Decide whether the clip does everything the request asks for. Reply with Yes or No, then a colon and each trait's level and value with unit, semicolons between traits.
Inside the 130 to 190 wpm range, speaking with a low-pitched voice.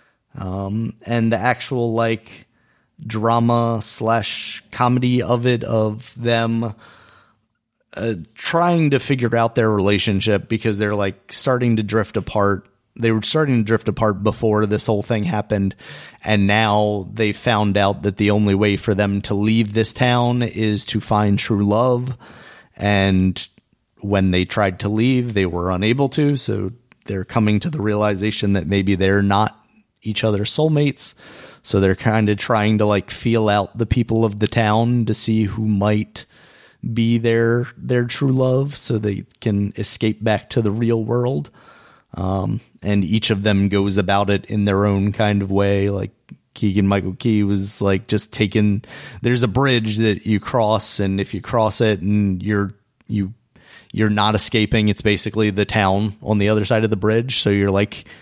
Yes: average, 170 wpm; low, 110 Hz